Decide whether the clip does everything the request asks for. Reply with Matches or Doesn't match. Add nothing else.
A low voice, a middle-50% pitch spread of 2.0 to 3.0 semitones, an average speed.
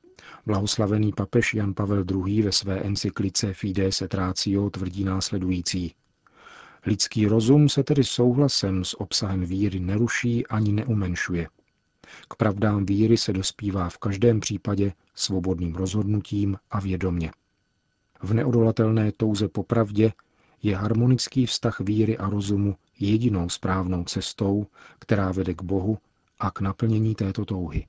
Matches